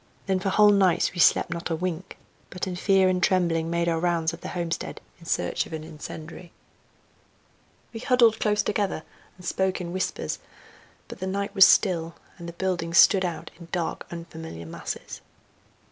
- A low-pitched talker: No, medium, 175 Hz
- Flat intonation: Yes, narrow, 2.3 semitones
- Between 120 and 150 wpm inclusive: No, average, 175 wpm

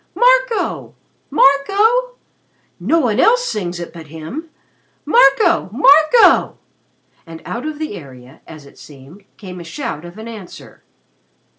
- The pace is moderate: No, slow, 125 wpm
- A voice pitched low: No, high, 220 Hz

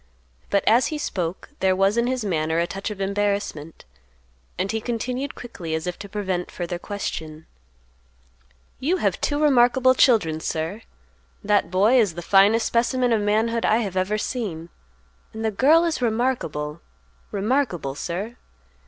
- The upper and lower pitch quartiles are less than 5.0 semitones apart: No, wide, 5.5 semitones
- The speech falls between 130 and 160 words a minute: Yes, average, 150 wpm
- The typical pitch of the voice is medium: No, high, 205 Hz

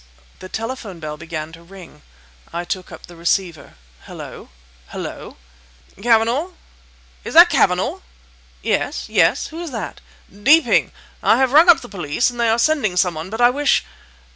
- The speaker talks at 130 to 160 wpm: Yes, average, 155 wpm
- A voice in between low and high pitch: No, high, 195 Hz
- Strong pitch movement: Yes, wide, 6.8 semitones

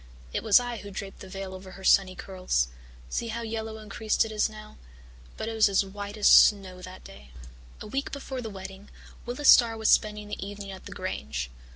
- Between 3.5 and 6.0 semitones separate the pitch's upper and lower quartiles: No, narrow, 2.5 semitones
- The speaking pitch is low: No, high, 205 Hz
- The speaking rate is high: Yes, fast, 215 wpm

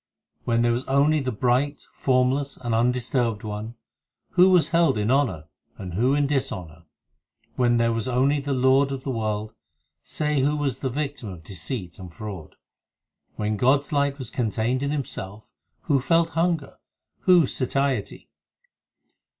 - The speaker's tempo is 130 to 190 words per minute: Yes, average, 160 wpm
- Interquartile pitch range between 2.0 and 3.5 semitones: No, average, 4.4 semitones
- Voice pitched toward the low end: Yes, low, 130 Hz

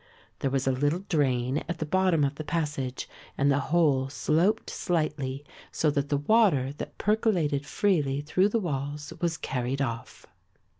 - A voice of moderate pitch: Yes, medium, 145 Hz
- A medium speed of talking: Yes, average, 160 wpm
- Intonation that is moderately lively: Yes, average, 3.9 semitones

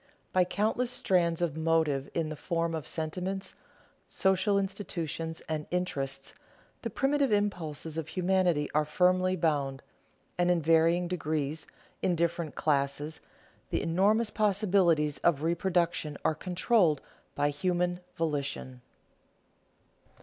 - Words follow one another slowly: Yes, slow, 115 wpm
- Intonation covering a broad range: No, average, 3.3 semitones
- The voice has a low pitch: No, medium, 170 Hz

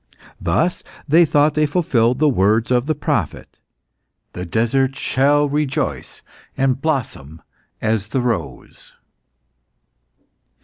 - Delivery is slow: Yes, slow, 105 wpm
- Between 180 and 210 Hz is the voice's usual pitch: No, low, 135 Hz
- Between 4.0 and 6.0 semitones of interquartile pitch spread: Yes, average, 4.7 semitones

